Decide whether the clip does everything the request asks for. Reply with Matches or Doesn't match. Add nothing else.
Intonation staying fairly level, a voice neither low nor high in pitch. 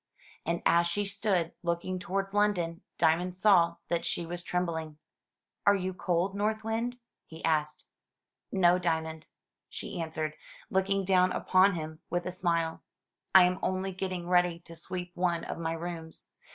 Matches